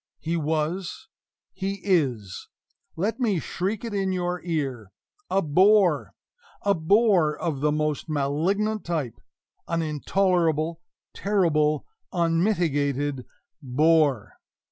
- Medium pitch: Yes, medium, 165 Hz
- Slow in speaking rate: Yes, slow, 100 wpm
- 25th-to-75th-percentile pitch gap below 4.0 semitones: No, average, 4.3 semitones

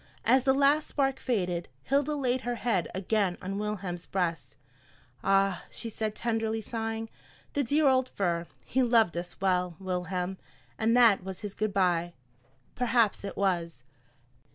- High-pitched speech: Yes, high, 205 Hz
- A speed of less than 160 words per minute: Yes, average, 150 wpm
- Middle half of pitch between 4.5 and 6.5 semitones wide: Yes, average, 5.0 semitones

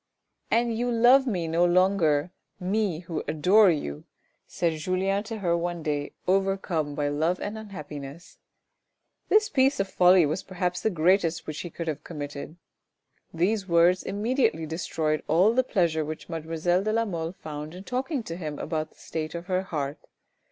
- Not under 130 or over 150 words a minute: No, average, 175 wpm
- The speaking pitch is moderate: Yes, medium, 175 Hz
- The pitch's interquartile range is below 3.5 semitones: No, average, 4.0 semitones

